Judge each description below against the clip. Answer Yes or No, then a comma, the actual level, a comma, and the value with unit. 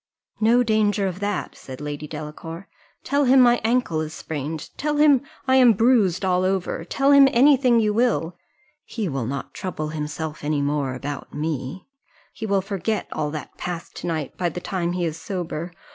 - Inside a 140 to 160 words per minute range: No, average, 185 wpm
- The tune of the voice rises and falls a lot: Yes, wide, 6.7 semitones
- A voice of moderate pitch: Yes, medium, 180 Hz